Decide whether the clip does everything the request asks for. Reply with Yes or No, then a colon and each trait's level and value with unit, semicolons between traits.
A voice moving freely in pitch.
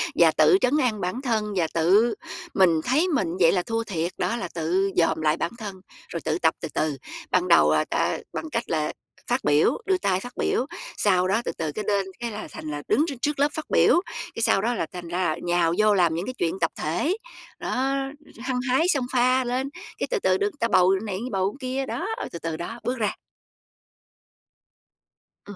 Yes: wide, 6.7 semitones